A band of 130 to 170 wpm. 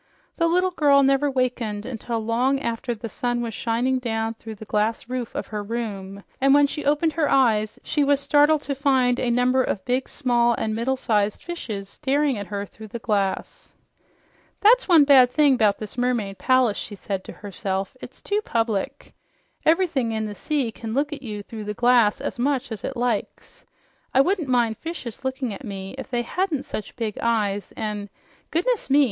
No: average, 190 wpm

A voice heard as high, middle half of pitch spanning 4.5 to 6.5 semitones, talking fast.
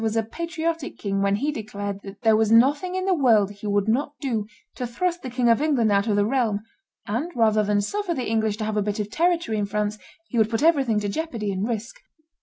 Yes: high, 225 Hz; average, 5.3 semitones; fast, 240 wpm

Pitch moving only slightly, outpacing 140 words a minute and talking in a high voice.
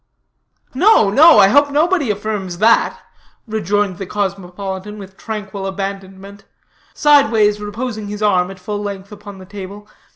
No: narrow, 1.9 semitones; slow, 135 wpm; high, 205 Hz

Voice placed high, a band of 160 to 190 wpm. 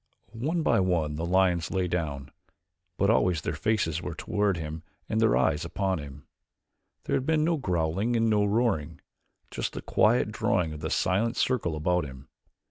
No: very low, 90 Hz; average, 175 wpm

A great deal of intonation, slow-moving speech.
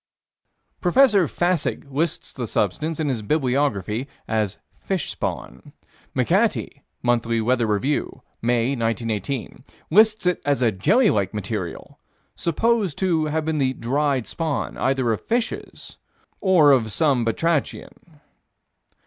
Yes: wide, 6.0 semitones; slow, 120 wpm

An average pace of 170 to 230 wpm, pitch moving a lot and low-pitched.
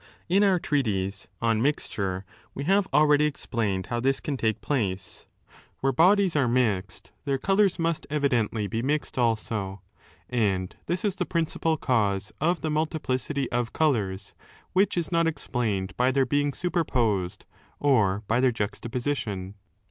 No: average, 150 wpm; wide, 6.5 semitones; low, 130 Hz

